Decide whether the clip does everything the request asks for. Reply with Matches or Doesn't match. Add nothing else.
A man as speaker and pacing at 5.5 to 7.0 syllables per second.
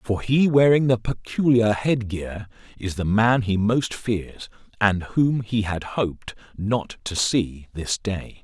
Doesn't match